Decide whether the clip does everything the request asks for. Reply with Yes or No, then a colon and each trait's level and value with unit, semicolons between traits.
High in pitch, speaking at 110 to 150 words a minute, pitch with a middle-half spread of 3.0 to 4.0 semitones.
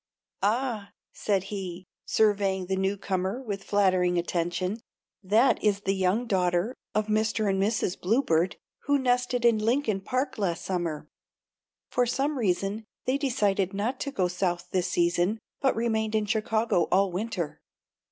Yes: high, 200 Hz; average, 145 wpm; average, 3.6 semitones